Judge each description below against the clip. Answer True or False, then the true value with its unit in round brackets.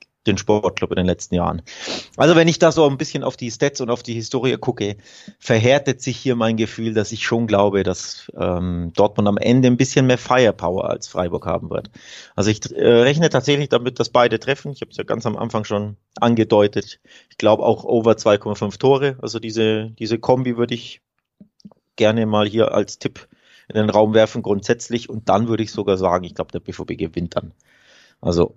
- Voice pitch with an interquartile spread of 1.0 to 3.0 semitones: False (3.7 semitones)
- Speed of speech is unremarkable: False (200 wpm)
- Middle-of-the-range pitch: False (115 Hz)